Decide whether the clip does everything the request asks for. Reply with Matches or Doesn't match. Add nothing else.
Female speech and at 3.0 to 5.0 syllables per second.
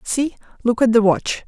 Matches